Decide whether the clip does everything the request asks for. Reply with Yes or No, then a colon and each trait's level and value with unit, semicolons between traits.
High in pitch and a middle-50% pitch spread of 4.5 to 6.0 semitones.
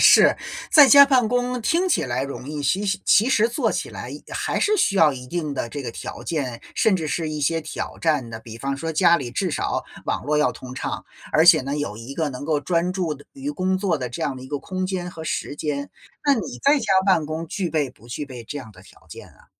No: medium, 155 Hz; wide, 5.6 semitones